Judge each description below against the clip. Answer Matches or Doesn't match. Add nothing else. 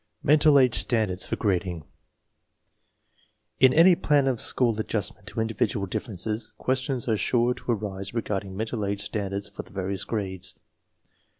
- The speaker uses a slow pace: Doesn't match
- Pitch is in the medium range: Doesn't match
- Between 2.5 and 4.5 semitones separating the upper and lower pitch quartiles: Matches